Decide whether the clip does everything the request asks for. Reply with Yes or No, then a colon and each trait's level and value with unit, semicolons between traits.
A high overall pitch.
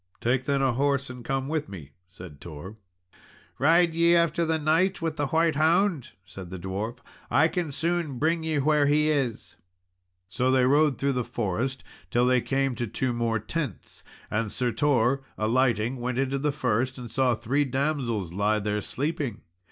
No: low, 130 Hz